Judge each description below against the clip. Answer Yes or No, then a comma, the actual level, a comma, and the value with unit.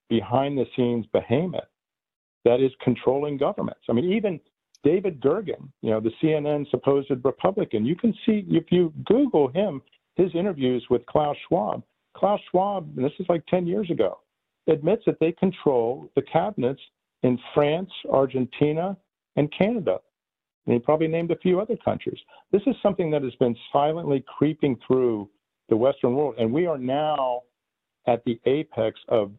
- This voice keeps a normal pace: Yes, average, 160 wpm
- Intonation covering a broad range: Yes, wide, 6.0 semitones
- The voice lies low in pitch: No, medium, 150 Hz